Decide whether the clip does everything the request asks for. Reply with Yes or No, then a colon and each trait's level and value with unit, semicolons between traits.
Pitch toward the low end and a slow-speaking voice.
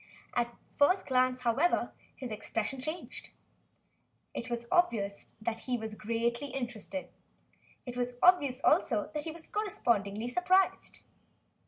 No: very high, 250 Hz; slow, 130 wpm